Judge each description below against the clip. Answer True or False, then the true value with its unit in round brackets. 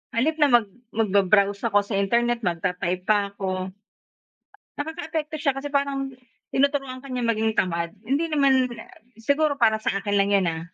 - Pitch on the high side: True (230 Hz)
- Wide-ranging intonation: True (5.9 semitones)